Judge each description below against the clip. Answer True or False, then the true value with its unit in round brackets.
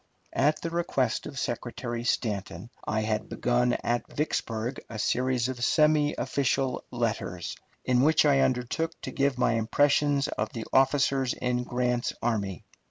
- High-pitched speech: False (125 Hz)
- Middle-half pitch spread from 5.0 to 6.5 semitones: False (3.0 semitones)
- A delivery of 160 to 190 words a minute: False (145 wpm)